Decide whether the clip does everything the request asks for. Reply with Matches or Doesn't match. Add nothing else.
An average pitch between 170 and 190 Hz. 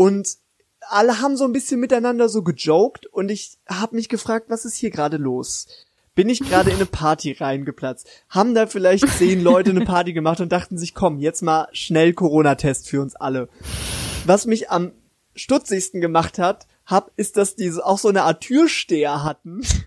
Matches